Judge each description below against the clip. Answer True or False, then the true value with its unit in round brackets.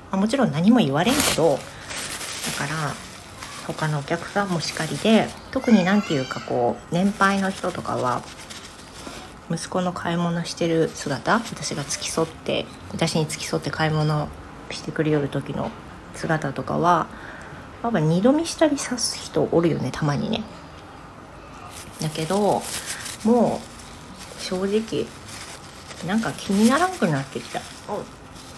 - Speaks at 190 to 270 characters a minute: True (255 characters per minute)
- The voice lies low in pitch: False (175 Hz)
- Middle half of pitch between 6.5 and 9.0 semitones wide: False (5.3 semitones)